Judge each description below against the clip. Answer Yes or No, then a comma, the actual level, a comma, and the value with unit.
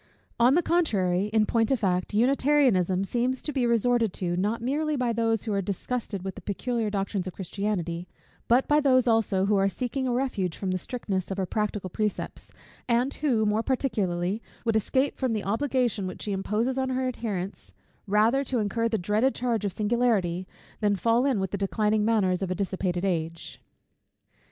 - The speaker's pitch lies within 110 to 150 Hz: No, high, 215 Hz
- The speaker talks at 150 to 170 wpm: No, average, 185 wpm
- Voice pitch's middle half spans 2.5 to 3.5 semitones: No, average, 4.3 semitones